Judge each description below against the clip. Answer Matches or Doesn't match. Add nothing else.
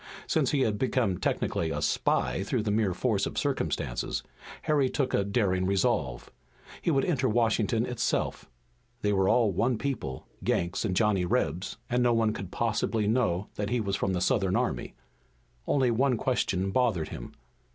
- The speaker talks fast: Doesn't match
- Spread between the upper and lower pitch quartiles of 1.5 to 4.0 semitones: Doesn't match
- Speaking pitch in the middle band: Doesn't match